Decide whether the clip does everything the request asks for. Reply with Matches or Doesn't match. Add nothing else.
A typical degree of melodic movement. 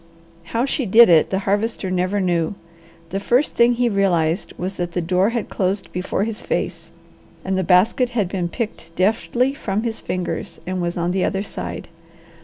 Matches